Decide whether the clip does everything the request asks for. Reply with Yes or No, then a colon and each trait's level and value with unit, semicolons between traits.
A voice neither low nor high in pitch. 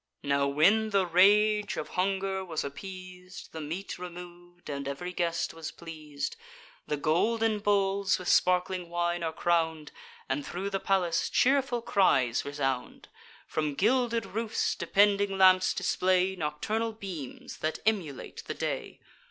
Yes: medium, 180 Hz